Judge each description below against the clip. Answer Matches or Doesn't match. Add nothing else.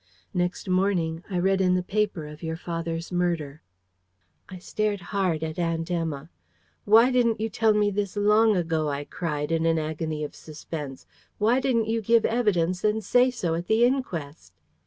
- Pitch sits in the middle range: Matches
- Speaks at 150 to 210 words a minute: Matches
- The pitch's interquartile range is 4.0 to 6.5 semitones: Matches